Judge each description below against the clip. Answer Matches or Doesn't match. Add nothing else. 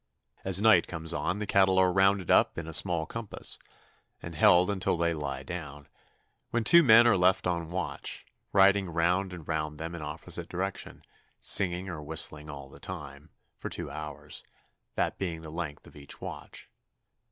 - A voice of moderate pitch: Doesn't match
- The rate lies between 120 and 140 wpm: Doesn't match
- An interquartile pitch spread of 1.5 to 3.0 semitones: Doesn't match